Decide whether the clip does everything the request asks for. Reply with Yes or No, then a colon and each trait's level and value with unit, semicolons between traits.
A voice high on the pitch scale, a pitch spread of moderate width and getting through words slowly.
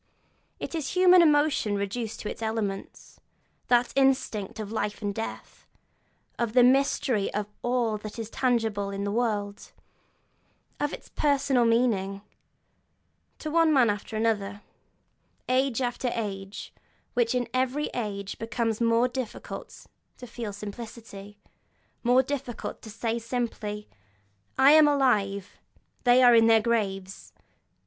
Yes: high, 230 Hz; average, 3.5 semitones; slow, 130 wpm